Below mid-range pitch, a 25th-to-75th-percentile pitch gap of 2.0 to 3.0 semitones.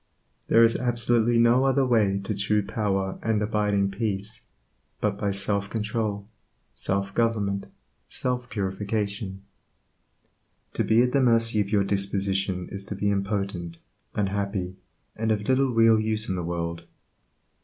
Yes: low, 105 Hz; narrow, 2.6 semitones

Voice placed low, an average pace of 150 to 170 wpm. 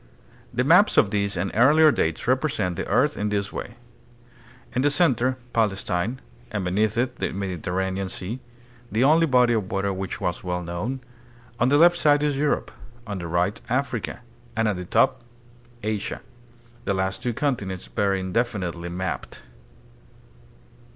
Yes: low, 105 Hz; average, 155 wpm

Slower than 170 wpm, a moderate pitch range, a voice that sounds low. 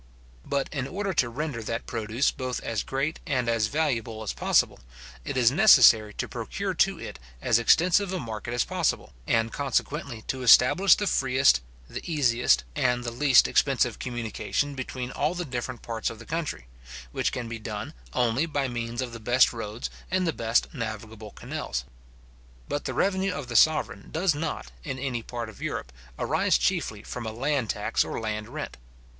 No: average, 180 wpm; average, 4.1 semitones; low, 125 Hz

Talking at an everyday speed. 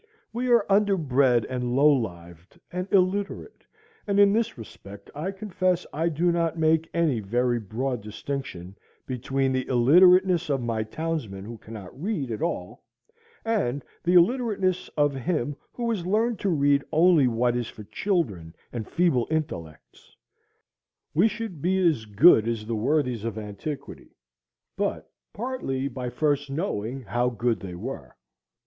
Yes: average, 145 wpm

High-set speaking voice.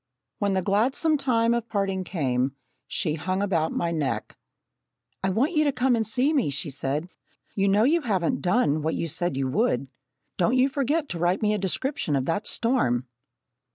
Yes: high, 195 Hz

